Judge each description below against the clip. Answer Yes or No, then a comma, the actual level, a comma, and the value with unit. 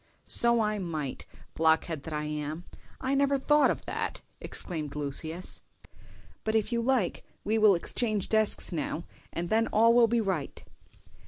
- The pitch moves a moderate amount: No, wide, 6.4 semitones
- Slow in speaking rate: No, average, 155 wpm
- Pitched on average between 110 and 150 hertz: No, high, 200 Hz